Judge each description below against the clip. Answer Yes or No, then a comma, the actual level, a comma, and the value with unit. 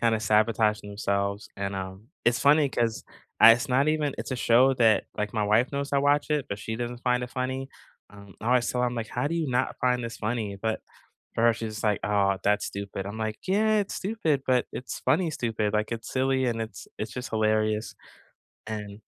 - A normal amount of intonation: Yes, average, 3.6 semitones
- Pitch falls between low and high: No, low, 115 Hz